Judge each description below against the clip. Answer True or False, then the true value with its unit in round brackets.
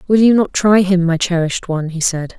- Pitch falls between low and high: True (180 Hz)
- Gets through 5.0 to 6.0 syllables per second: True (5.9 syllables/s)